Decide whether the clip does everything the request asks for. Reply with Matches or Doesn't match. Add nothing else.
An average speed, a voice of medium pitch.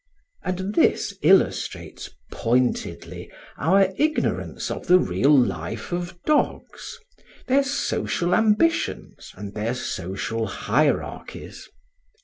Doesn't match